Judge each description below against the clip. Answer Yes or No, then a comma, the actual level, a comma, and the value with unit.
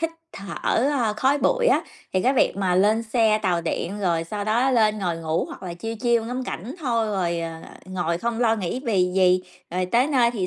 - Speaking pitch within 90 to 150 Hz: No, high, 215 Hz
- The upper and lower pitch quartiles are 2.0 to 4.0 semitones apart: No, average, 4.6 semitones